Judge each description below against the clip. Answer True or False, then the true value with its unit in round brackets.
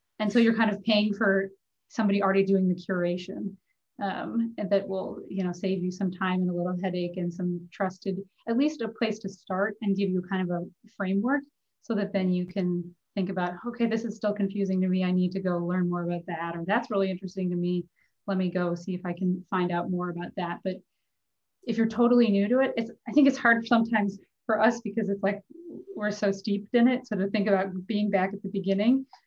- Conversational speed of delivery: False (235 wpm)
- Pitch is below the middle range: False (195 Hz)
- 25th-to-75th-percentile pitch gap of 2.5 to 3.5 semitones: True (3.1 semitones)